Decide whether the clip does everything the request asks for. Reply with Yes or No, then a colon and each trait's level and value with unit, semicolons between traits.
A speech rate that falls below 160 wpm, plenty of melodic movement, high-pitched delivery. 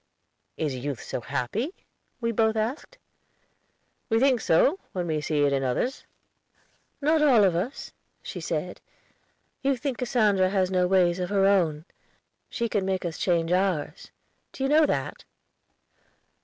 Yes: average, 150 wpm; wide, 6.5 semitones; high, 195 Hz